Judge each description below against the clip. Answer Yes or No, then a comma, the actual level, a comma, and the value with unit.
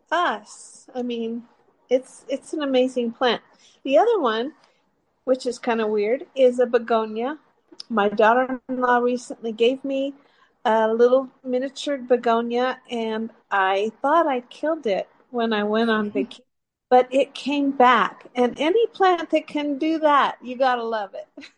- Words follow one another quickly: No, average, 155 wpm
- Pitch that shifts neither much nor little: Yes, average, 3.2 semitones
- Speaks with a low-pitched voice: No, very high, 250 Hz